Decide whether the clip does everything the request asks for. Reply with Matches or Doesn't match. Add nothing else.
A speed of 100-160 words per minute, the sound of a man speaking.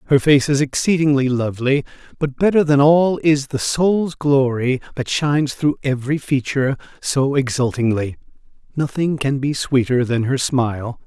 Matches